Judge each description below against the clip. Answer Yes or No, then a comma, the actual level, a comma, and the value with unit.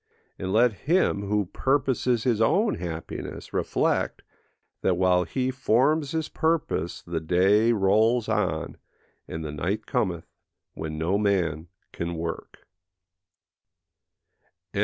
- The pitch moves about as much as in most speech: No, wide, 6.3 semitones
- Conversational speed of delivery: No, slow, 115 wpm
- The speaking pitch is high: No, low, 100 Hz